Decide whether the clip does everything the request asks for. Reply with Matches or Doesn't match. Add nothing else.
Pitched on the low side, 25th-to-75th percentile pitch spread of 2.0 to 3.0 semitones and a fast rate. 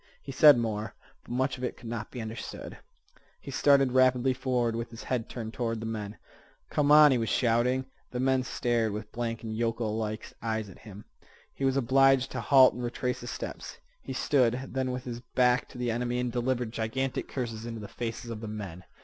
Matches